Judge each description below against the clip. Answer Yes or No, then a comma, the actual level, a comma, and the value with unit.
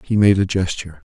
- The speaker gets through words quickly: Yes, fast, 215 wpm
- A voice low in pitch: Yes, very low, 95 Hz